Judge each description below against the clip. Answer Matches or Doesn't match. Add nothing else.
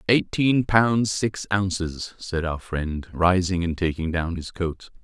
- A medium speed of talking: Matches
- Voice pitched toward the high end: Doesn't match